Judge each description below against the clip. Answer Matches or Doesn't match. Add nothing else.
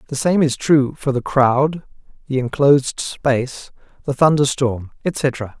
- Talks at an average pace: Matches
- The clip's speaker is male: Matches